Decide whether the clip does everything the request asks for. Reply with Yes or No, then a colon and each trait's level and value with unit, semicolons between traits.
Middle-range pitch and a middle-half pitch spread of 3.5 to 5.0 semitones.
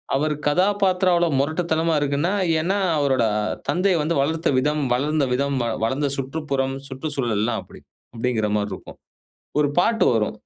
Yes: medium, 145 Hz; average, 3.9 semitones